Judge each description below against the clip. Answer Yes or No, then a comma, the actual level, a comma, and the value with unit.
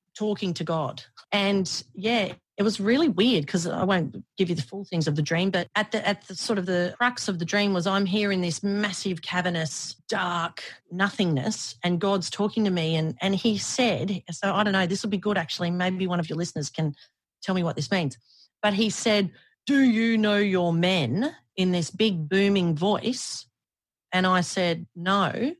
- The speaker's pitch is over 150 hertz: Yes, high, 190 Hz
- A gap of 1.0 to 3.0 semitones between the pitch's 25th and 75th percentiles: No, average, 3.4 semitones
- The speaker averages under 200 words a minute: No, fast, 205 wpm